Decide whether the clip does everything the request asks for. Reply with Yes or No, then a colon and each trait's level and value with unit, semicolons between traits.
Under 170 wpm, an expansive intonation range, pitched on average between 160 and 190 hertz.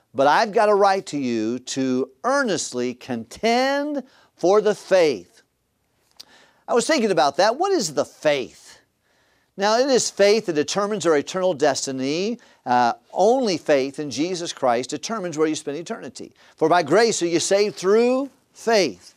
Yes: average, 155 wpm; wide, 8.4 semitones; medium, 185 Hz